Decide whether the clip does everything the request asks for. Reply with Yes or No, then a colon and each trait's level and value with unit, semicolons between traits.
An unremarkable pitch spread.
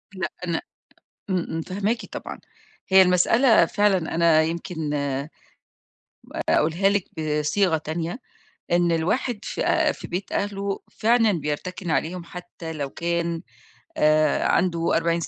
Yes: average, 3.2 semitones